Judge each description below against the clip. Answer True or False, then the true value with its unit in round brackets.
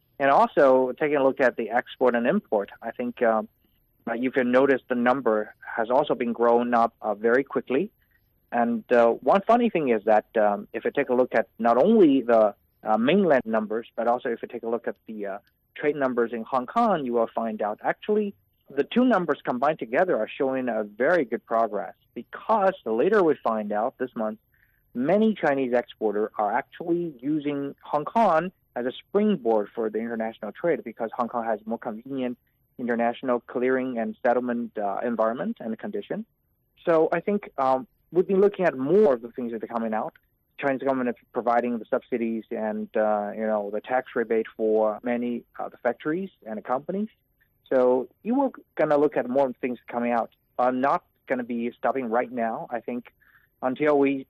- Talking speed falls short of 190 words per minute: False (195 wpm)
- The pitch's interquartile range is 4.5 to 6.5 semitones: False (3.7 semitones)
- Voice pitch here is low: True (125 Hz)